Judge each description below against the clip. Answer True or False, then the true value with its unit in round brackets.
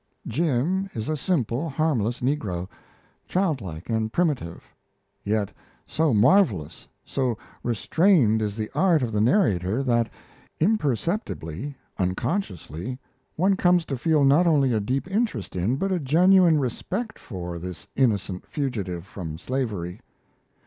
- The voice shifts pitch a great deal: True (8.1 semitones)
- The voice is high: False (130 Hz)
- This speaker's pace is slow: True (125 wpm)